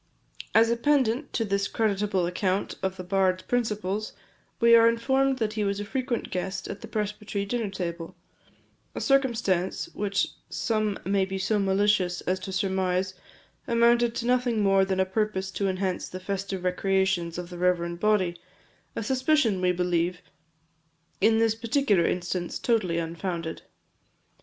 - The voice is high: Yes, high, 195 Hz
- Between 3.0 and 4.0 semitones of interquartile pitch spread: Yes, average, 3.5 semitones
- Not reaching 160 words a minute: Yes, average, 150 wpm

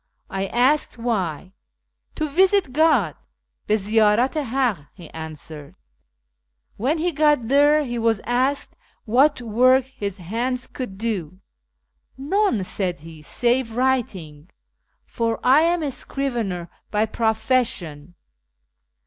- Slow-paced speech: Yes, slow, 130 wpm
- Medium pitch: No, high, 230 Hz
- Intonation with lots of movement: Yes, wide, 5.9 semitones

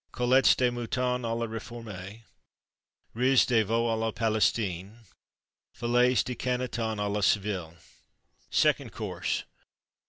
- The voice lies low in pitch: Yes, low, 115 Hz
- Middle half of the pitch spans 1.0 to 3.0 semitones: Yes, narrow, 2.5 semitones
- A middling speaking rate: No, slow, 120 wpm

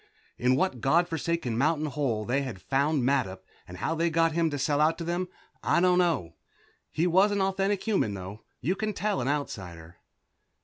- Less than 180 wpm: No, average, 190 wpm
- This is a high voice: No, medium, 155 Hz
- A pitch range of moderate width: No, wide, 6.1 semitones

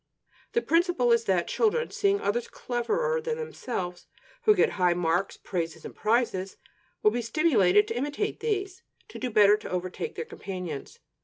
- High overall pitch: Yes, high, 235 Hz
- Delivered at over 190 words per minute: No, average, 160 wpm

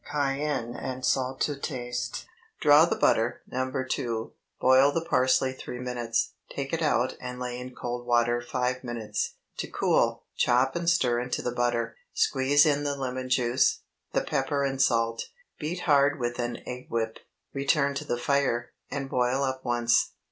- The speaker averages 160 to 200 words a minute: Yes, average, 165 wpm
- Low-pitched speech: Yes, low, 130 Hz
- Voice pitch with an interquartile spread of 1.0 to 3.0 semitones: Yes, narrow, 2.4 semitones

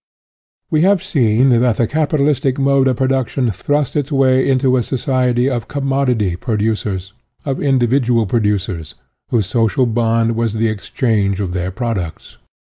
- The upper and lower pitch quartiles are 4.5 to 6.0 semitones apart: No, average, 3.7 semitones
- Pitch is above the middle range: No, low, 120 Hz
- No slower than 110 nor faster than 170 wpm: Yes, average, 150 wpm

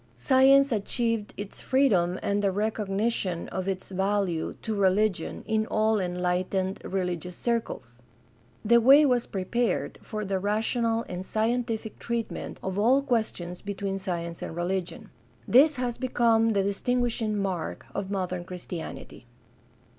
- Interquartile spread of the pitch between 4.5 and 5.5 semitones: No, average, 3.9 semitones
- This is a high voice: Yes, high, 205 Hz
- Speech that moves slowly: Yes, slow, 130 wpm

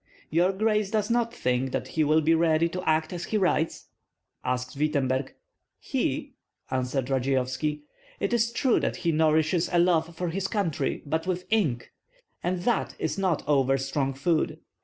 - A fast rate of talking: No, average, 165 wpm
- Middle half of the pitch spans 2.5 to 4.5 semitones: No, average, 5.0 semitones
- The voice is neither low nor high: Yes, medium, 160 Hz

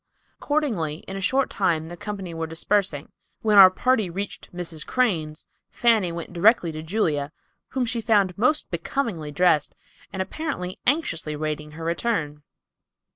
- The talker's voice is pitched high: No, medium, 180 Hz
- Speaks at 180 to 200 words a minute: No, average, 145 wpm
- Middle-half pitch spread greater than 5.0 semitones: Yes, wide, 5.6 semitones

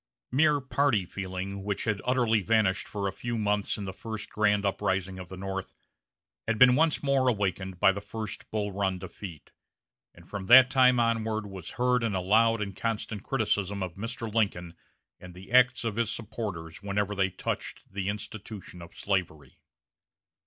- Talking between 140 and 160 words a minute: No, average, 170 wpm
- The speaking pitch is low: Yes, low, 105 Hz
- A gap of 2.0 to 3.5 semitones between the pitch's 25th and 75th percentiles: Yes, average, 3.2 semitones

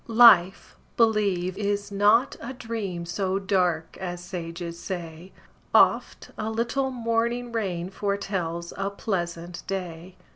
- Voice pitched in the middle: No, high, 195 Hz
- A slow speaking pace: Yes, slow, 115 wpm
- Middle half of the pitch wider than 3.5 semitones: Yes, average, 4.1 semitones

